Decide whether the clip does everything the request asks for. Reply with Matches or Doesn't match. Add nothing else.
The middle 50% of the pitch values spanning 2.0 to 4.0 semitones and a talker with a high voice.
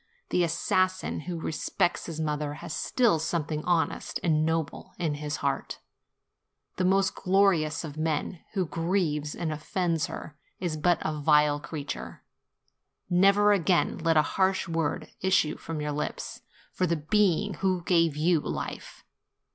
Doesn't match